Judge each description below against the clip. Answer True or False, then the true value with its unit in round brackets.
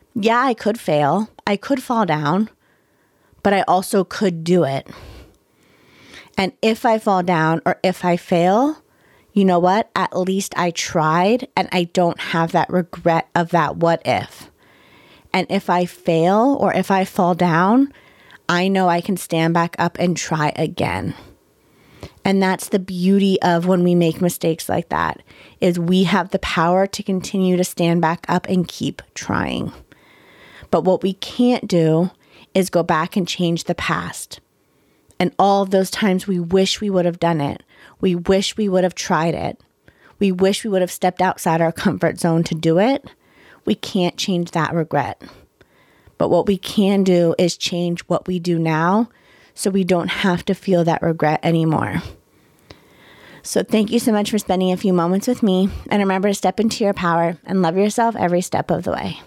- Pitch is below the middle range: False (185 Hz)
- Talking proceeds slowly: False (180 wpm)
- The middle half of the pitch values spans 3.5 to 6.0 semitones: False (2.5 semitones)